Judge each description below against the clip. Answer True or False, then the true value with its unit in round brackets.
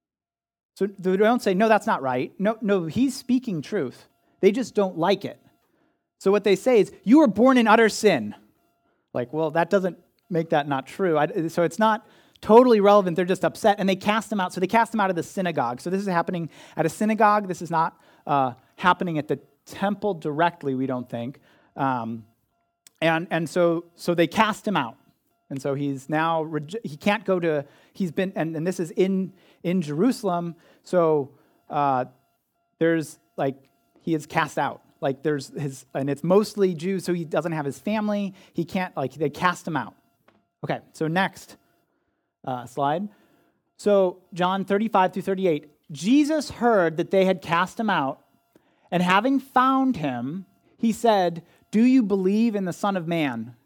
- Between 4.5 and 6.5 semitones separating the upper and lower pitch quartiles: True (5.0 semitones)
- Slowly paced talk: False (180 wpm)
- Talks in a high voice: False (180 Hz)